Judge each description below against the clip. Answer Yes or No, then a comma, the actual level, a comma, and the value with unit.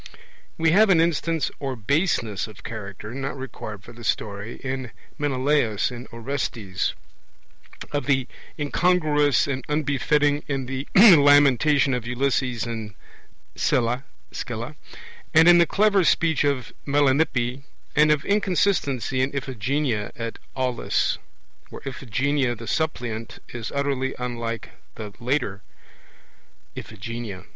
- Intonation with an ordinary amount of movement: Yes, average, 3.9 semitones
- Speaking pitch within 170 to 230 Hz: No, low, 135 Hz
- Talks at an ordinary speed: No, slow, 120 wpm